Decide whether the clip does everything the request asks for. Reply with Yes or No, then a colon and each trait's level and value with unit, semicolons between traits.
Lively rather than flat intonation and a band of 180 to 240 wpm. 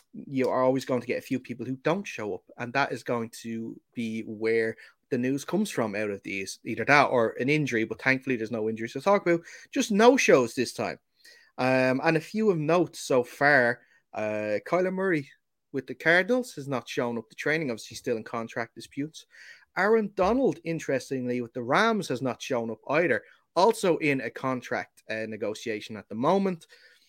Yes: wide, 7.2 semitones; average, 200 wpm